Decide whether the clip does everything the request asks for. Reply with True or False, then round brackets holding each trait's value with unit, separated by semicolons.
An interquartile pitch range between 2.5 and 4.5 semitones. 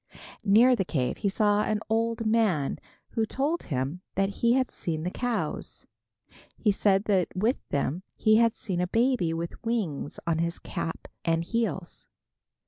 False (5.2 semitones)